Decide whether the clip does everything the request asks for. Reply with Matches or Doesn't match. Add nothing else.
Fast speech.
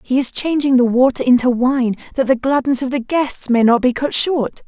Matches